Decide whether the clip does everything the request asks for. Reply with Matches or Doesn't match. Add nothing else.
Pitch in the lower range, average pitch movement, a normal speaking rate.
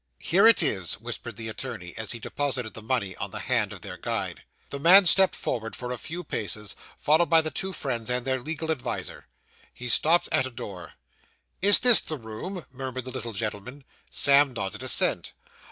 Doesn't match